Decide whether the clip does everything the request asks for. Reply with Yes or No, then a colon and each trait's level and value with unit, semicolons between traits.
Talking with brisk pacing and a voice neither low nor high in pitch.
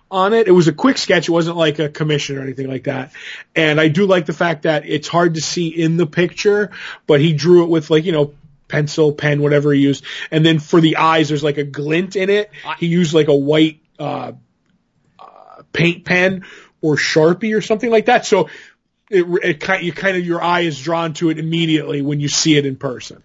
Yes: fast, 230 wpm; medium, 160 Hz